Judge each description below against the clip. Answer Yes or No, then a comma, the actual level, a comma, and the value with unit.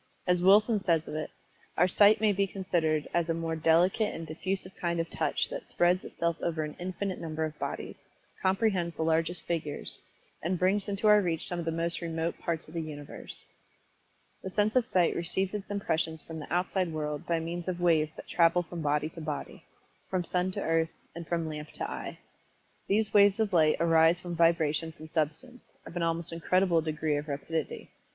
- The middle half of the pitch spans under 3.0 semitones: Yes, narrow, 2.6 semitones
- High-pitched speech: No, medium, 170 Hz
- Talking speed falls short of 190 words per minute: No, average, 195 wpm